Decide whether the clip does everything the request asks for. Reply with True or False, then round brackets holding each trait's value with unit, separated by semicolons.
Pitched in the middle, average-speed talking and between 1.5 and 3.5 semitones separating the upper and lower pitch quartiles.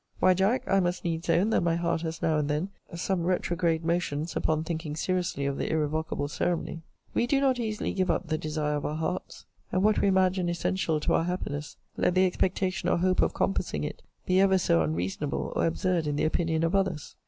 False (170 Hz; 210 wpm; 3.1 semitones)